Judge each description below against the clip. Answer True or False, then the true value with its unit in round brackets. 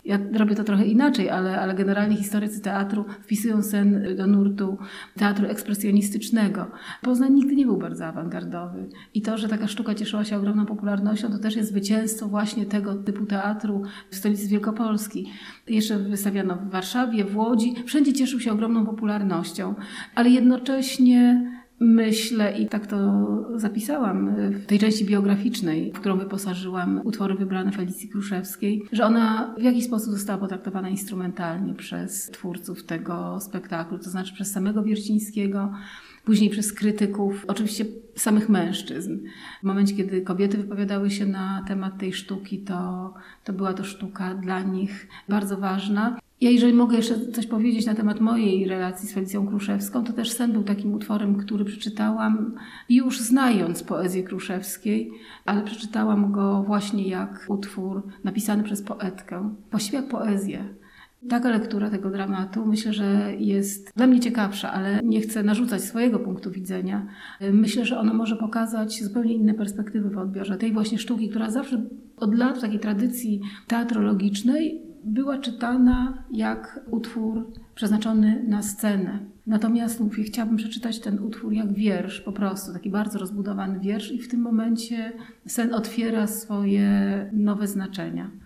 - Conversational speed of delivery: True (150 wpm)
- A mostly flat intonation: True (2.2 semitones)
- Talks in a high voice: True (210 Hz)